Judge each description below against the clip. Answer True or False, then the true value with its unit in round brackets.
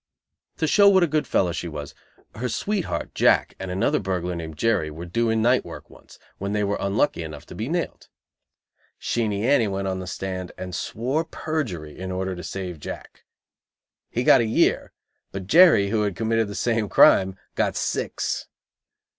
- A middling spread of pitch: True (4.4 semitones)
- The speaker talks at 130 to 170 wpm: False (180 wpm)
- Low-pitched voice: True (100 Hz)